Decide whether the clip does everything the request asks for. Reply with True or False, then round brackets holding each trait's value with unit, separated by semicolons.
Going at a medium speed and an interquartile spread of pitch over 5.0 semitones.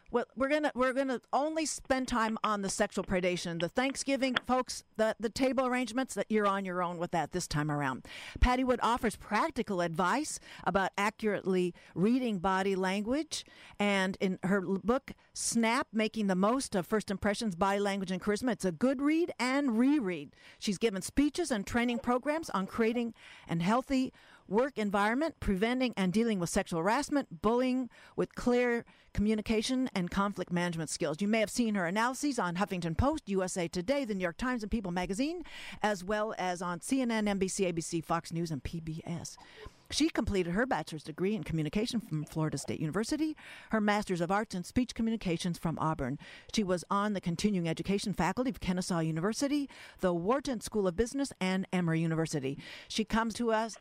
True (175 wpm; 5.4 semitones)